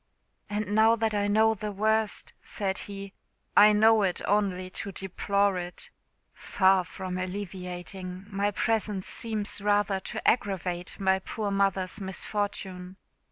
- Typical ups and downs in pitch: No, narrow, 2.0 semitones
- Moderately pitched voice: No, high, 200 Hz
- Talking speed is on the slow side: Yes, slow, 125 wpm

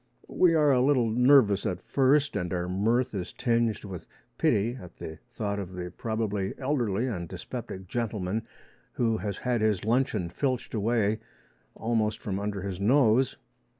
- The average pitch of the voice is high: No, low, 110 Hz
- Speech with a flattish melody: No, average, 3.9 semitones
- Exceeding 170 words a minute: No, average, 155 wpm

